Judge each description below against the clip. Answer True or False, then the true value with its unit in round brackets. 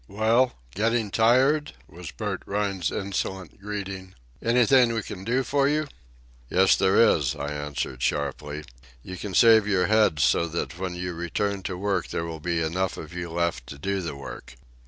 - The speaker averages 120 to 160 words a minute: False (175 wpm)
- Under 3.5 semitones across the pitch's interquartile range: False (4.5 semitones)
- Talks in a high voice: False (95 Hz)